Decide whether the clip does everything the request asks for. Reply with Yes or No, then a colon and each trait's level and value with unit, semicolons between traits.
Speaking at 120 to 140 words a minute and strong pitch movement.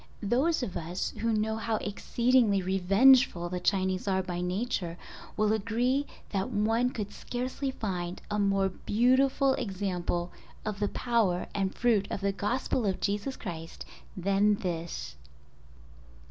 No: slow, 135 wpm; average, 4.2 semitones